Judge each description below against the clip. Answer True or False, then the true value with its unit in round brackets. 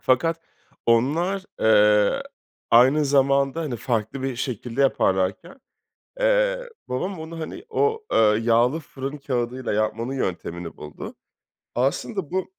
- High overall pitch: False (135 Hz)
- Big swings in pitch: True (6.1 semitones)